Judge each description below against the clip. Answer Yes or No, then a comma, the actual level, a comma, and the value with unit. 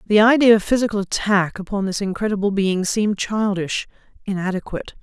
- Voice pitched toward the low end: No, high, 200 Hz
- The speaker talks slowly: Yes, slow, 130 wpm